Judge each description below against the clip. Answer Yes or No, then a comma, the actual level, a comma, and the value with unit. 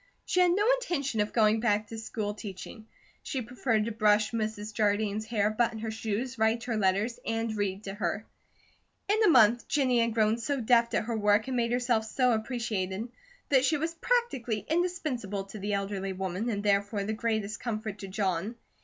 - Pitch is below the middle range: No, high, 220 Hz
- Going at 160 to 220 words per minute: Yes, average, 190 wpm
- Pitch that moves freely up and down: No, average, 2.7 semitones